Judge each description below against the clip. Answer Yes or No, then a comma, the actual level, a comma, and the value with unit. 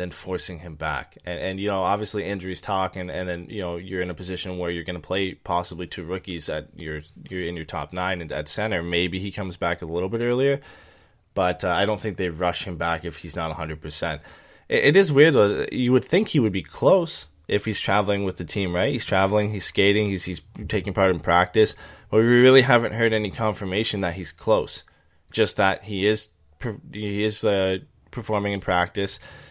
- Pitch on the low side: Yes, very low, 95 Hz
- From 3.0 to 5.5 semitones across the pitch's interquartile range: Yes, average, 3.3 semitones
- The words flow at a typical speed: No, fast, 220 wpm